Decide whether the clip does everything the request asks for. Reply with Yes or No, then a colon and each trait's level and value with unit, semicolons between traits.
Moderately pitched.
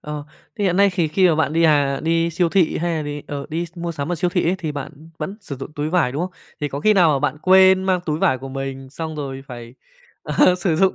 Yes: medium, 160 Hz